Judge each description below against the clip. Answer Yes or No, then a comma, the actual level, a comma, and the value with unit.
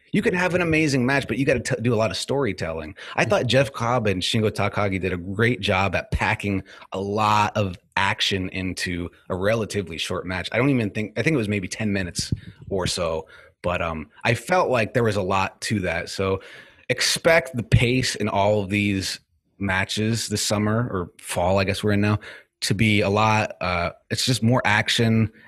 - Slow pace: No, fast, 205 wpm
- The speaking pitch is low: Yes, low, 105 Hz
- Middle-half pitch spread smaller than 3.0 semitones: No, average, 3.5 semitones